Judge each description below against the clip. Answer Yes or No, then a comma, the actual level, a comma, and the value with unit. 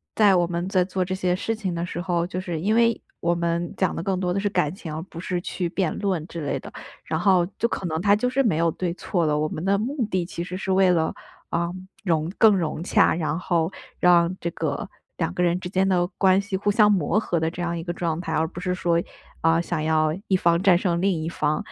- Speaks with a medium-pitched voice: Yes, medium, 175 Hz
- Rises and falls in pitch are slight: Yes, narrow, 2.2 semitones